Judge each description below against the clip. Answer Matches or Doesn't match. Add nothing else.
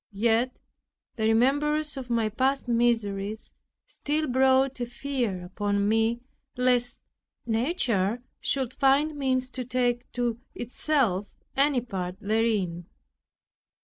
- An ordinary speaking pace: Doesn't match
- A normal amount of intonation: Matches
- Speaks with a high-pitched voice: Matches